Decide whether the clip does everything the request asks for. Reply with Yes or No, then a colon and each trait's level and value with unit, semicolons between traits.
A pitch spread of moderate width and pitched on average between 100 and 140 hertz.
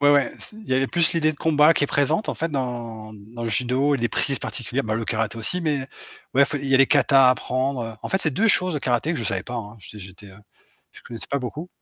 Yes: average, 4.4 semitones; low, 130 Hz